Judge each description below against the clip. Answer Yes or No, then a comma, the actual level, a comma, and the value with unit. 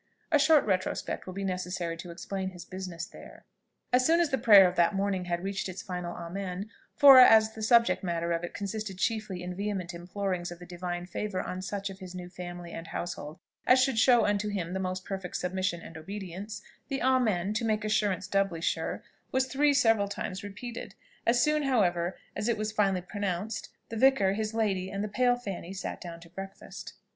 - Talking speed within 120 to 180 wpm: No, average, 200 wpm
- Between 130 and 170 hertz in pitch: No, high, 195 Hz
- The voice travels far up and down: No, average, 3.4 semitones